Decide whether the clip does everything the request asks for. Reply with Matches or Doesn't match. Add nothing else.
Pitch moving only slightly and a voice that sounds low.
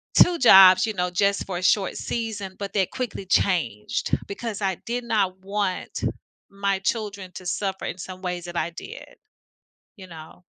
Doesn't match